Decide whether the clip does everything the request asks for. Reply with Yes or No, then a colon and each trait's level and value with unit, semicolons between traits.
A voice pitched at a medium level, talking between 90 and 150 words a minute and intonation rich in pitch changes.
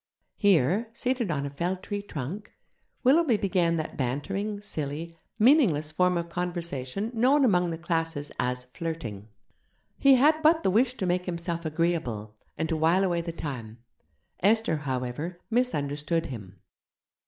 Yes: medium, 170 Hz; average, 140 wpm; wide, 5.7 semitones